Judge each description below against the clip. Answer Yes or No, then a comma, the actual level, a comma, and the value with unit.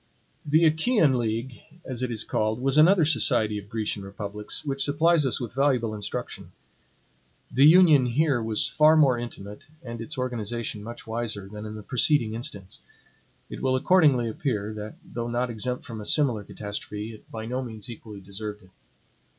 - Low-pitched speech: Yes, low, 120 Hz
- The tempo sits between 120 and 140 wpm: No, average, 170 wpm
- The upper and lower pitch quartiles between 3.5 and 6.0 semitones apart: Yes, average, 4.1 semitones